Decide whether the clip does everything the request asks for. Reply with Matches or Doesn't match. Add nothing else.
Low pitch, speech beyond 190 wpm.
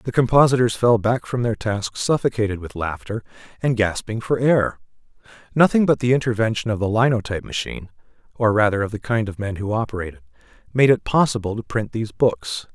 Doesn't match